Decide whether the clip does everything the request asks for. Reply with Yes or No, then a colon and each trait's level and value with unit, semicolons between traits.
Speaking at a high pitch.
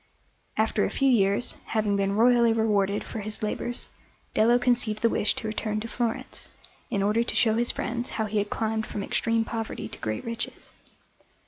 Yes: high, 220 Hz